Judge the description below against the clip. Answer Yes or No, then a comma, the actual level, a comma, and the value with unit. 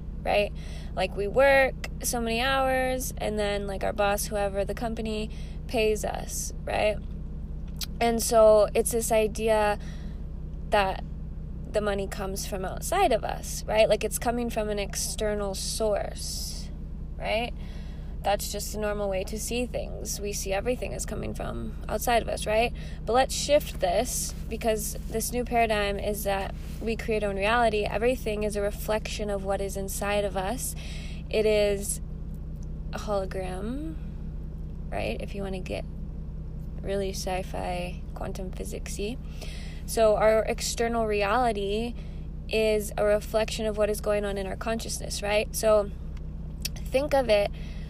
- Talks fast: No, average, 150 wpm